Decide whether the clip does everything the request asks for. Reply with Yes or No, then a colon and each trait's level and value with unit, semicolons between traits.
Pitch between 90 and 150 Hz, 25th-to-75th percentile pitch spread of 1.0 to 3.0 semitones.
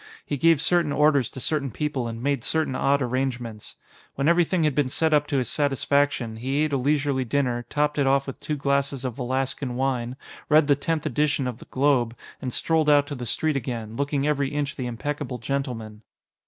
Yes: medium, 140 Hz; average, 2.7 semitones